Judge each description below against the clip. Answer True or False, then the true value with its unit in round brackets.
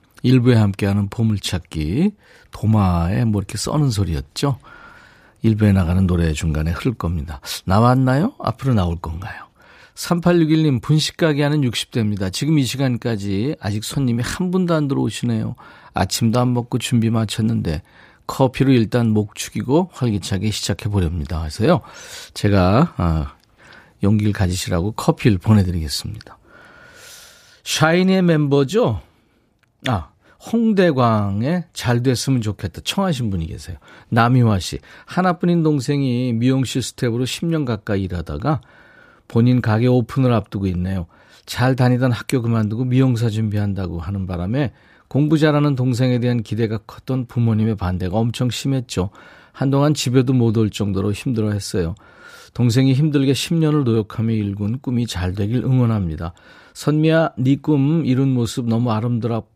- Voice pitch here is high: False (115 Hz)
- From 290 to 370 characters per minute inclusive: True (315 characters per minute)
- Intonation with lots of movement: False (4.8 semitones)